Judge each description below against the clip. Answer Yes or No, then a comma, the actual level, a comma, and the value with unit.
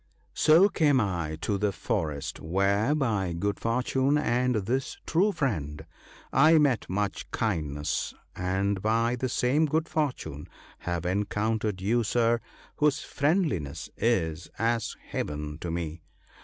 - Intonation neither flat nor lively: No, wide, 7.0 semitones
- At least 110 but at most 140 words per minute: Yes, slow, 135 wpm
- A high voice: No, low, 105 Hz